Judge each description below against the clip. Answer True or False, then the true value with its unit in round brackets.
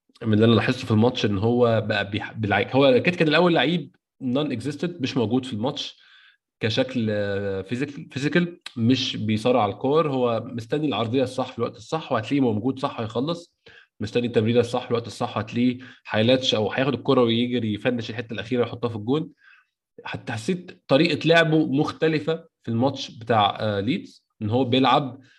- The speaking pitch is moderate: False (125 Hz)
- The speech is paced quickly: True (160 wpm)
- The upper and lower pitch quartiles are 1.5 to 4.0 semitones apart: True (3.7 semitones)